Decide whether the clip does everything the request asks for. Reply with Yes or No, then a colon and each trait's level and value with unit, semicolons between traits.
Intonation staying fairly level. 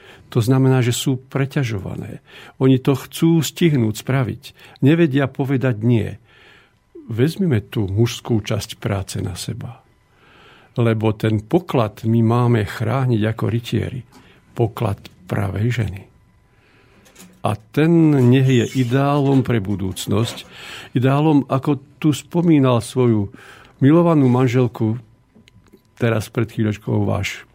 No: average, 3.4 semitones